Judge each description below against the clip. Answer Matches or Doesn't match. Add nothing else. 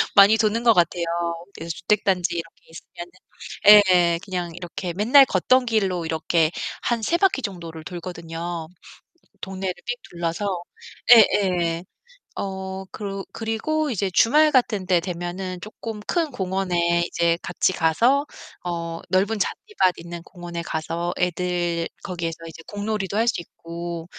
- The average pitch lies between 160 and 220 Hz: Matches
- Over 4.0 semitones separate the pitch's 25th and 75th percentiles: Doesn't match